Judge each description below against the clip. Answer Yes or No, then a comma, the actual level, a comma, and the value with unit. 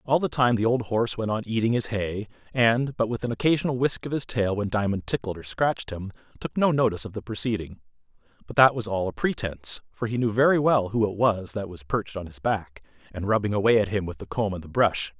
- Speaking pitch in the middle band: No, low, 110 Hz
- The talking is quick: Yes, fast, 250 wpm